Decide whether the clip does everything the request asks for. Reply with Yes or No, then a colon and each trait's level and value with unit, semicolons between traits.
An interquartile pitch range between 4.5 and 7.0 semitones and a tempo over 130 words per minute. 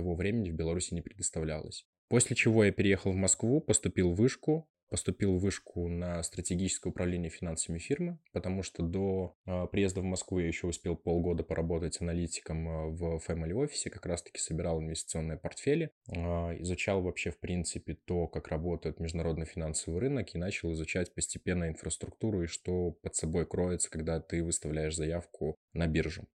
No: average, 2.7 semitones; fast, 160 wpm